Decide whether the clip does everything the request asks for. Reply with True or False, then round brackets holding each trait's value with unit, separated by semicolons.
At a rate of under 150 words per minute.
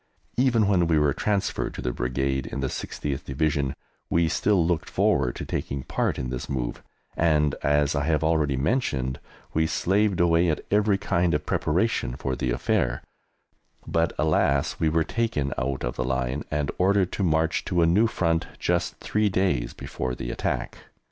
False (175 wpm)